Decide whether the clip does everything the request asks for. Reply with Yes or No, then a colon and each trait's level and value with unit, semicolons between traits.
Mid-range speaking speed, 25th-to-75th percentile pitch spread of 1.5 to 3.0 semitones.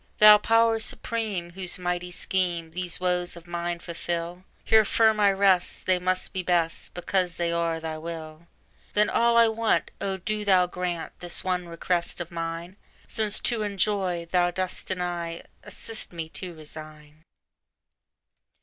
Yes: average, 150 wpm; narrow, 2.6 semitones